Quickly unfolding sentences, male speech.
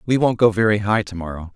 Yes: fast, 270 wpm; male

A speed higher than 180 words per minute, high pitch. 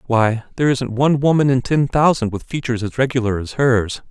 No: fast, 205 wpm; low, 125 Hz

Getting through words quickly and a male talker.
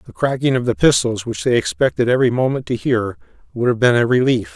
Yes: fast, 225 wpm; male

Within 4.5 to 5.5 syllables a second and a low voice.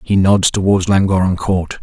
Yes: 4.7 syllables/s; very low, 95 Hz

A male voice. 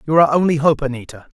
Yes: male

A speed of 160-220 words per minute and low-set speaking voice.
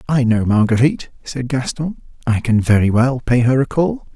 Yes: average, 190 wpm; low, 130 Hz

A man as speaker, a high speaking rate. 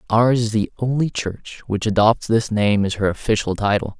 No: male; average, 195 wpm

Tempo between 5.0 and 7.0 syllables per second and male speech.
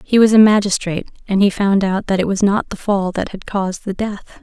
No: 5.5 syllables/s; female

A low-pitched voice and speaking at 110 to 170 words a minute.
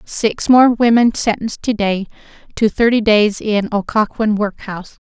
No: high, 215 Hz; average, 140 wpm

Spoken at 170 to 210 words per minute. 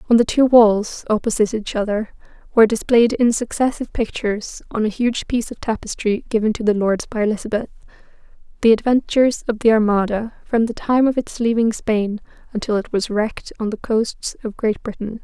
Yes: average, 180 wpm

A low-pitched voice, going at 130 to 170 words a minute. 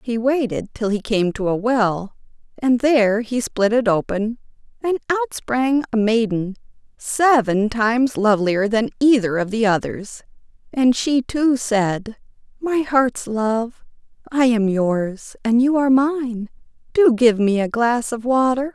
No: high, 235 Hz; average, 155 wpm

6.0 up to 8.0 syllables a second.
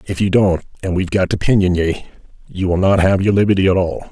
Yes: 6.3 syllables/s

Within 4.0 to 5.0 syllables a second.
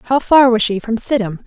Yes: 4.9 syllables/s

